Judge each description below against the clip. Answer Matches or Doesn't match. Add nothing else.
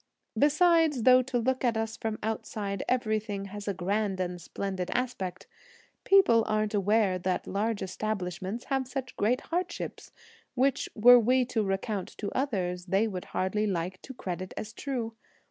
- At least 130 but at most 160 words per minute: Matches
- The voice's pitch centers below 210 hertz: Doesn't match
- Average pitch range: Matches